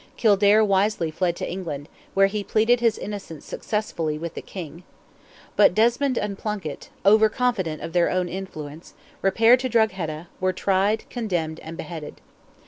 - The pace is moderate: Yes, average, 150 wpm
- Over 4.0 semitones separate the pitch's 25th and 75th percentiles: Yes, average, 4.4 semitones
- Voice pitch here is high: Yes, high, 195 Hz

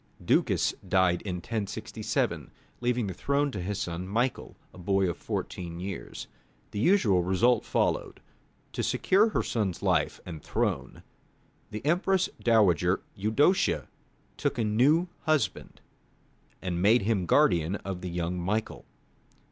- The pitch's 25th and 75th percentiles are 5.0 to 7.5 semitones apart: Yes, average, 5.3 semitones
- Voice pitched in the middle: No, low, 100 Hz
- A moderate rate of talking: No, slow, 130 wpm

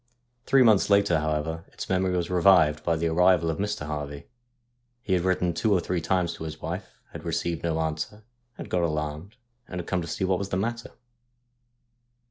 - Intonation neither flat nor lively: Yes, average, 3.0 semitones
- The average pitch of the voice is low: Yes, very low, 90 Hz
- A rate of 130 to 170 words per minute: No, average, 195 wpm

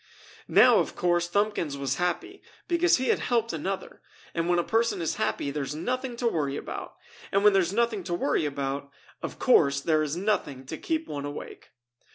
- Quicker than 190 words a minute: Yes, average, 200 wpm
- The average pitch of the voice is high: No, medium, 175 Hz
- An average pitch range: No, wide, 7.6 semitones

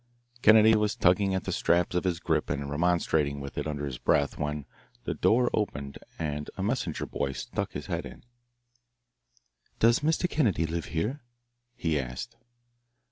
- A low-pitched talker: Yes, very low, 85 Hz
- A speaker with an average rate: Yes, average, 160 wpm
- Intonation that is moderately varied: No, wide, 6.6 semitones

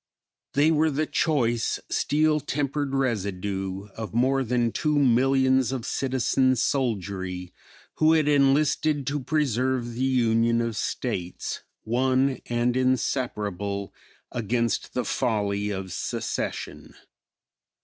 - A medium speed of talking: No, slow, 110 wpm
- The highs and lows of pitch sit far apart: No, average, 3.9 semitones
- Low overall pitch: Yes, low, 125 Hz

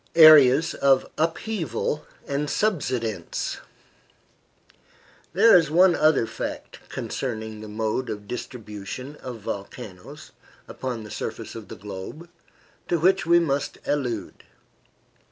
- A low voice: Yes, low, 130 Hz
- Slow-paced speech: Yes, slow, 110 wpm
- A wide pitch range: Yes, wide, 6.4 semitones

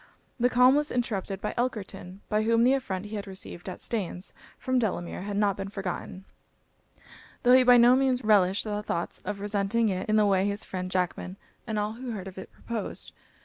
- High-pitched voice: Yes, high, 210 Hz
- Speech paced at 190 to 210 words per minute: Yes, average, 200 wpm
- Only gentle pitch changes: No, average, 3.6 semitones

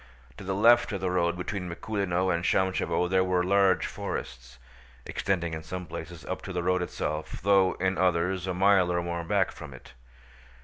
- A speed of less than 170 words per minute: No, average, 185 wpm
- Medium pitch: No, very low, 90 Hz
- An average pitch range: No, narrow, 1.7 semitones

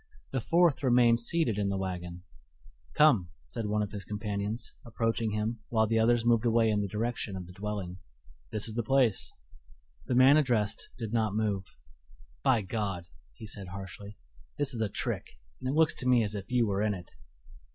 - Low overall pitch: Yes, low, 110 Hz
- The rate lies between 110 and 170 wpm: No, average, 190 wpm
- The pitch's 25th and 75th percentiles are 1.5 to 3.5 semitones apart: Yes, average, 3.0 semitones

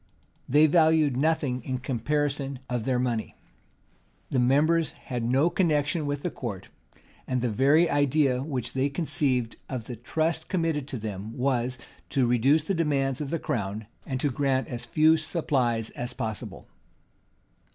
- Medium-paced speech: Yes, average, 150 wpm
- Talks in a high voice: No, low, 135 Hz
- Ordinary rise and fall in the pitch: Yes, average, 3.7 semitones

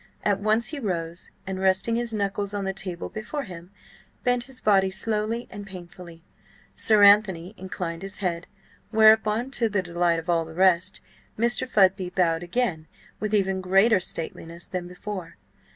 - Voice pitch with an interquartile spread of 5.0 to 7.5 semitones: No, average, 3.5 semitones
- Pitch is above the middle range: Yes, high, 195 Hz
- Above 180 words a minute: No, average, 160 wpm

